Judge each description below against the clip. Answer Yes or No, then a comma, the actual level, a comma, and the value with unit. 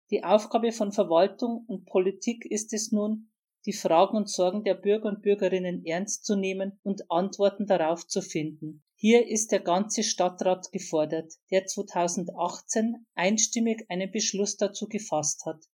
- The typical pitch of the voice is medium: No, high, 200 Hz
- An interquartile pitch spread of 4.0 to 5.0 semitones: No, average, 3.0 semitones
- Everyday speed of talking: Yes, average, 150 wpm